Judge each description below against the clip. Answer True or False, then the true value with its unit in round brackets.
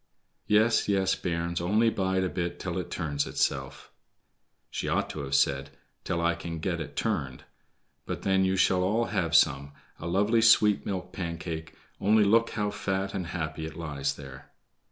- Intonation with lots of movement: False (3.8 semitones)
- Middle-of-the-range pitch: False (90 Hz)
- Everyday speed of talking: True (160 wpm)